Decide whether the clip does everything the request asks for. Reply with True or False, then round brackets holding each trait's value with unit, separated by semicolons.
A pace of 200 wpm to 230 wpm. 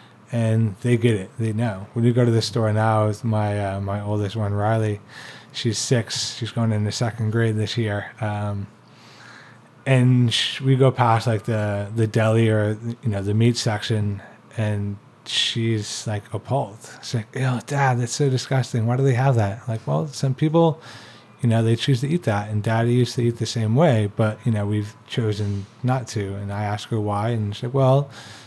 True (205 wpm)